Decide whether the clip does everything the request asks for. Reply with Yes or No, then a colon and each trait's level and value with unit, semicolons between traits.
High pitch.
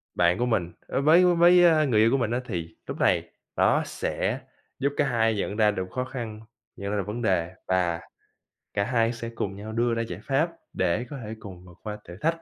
No: low, 110 Hz